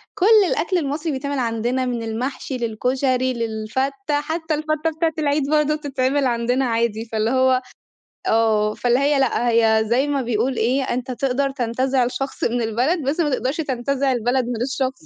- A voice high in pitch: Yes, very high, 260 Hz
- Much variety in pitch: No, average, 3.1 semitones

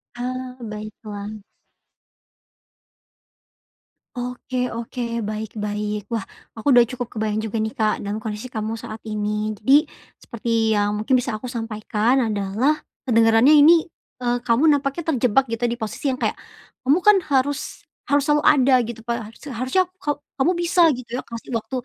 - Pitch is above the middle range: Yes, high, 235 Hz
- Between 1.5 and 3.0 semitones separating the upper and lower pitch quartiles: No, average, 3.5 semitones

